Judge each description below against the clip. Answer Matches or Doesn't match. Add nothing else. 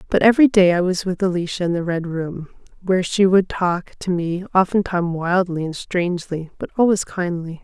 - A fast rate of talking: Doesn't match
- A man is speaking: Doesn't match